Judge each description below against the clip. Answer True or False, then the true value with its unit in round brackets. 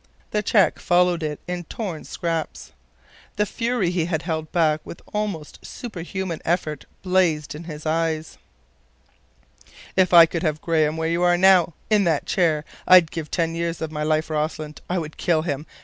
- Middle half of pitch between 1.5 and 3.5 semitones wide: True (2.5 semitones)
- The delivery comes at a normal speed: True (165 wpm)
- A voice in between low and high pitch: True (165 Hz)